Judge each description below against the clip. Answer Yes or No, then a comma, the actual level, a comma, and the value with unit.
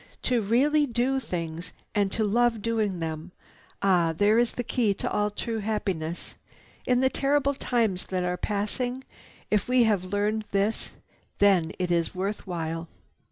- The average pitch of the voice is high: Yes, high, 205 Hz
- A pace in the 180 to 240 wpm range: No, average, 160 wpm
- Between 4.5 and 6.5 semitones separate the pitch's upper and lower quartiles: Yes, average, 4.8 semitones